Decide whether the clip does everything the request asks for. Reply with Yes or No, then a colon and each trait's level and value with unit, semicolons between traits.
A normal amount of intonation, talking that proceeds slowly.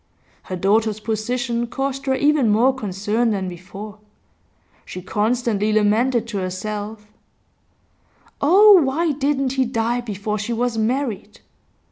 Yes: average, 3.9 semitones; slow, 120 wpm